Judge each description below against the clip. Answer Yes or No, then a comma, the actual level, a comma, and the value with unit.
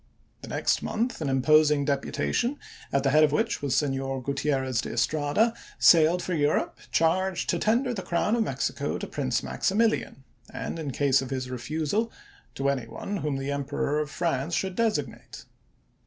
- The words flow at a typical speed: Yes, average, 170 wpm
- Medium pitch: Yes, medium, 150 Hz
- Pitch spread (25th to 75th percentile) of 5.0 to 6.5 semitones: Yes, wide, 5.5 semitones